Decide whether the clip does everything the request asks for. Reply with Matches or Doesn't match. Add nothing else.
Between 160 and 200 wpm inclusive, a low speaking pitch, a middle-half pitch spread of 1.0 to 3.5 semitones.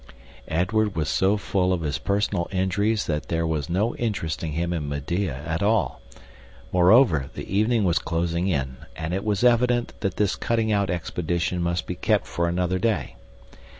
Doesn't match